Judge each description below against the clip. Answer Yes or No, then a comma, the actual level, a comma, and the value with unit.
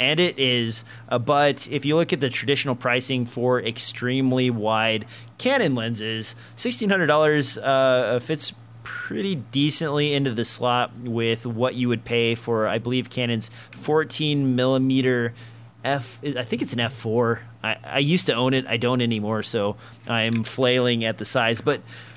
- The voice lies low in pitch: Yes, low, 125 Hz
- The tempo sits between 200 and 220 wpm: No, average, 165 wpm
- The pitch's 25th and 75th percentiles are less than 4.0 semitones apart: Yes, average, 2.8 semitones